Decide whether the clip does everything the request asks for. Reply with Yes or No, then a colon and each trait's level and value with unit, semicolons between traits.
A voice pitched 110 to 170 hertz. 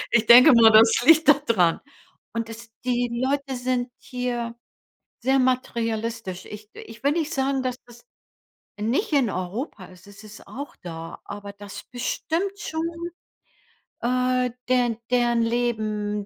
No: high, 240 Hz